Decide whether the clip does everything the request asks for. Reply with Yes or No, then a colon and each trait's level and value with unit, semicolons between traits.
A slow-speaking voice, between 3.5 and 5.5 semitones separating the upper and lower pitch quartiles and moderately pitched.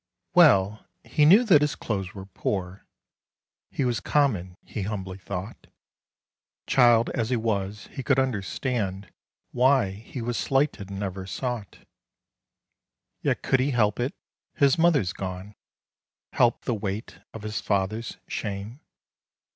No: slow, 130 wpm; average, 4.9 semitones; low, 110 Hz